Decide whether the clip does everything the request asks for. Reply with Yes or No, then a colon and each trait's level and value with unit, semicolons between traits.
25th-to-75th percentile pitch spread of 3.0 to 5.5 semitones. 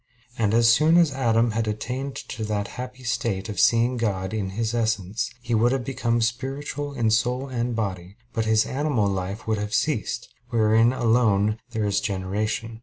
No: narrow, 2.6 semitones